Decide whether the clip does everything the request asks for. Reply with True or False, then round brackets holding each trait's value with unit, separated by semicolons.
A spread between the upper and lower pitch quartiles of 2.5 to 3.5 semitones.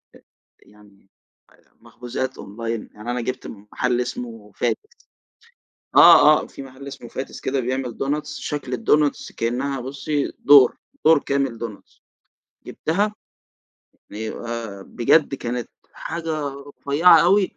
False (3.9 semitones)